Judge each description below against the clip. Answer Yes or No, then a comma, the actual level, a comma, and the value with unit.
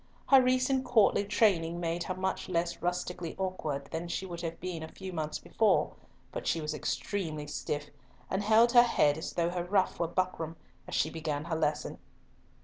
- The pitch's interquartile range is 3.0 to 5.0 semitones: Yes, average, 3.3 semitones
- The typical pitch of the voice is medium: Yes, medium, 175 Hz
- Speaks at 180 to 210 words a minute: Yes, average, 185 wpm